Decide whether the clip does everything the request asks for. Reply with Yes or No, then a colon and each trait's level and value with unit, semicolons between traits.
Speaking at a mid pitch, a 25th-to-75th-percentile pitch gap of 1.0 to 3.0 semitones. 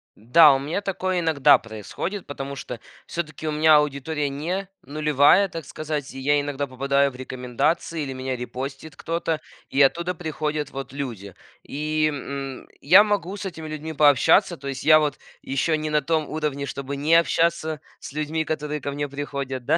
Yes: medium, 150 Hz; narrow, 2.6 semitones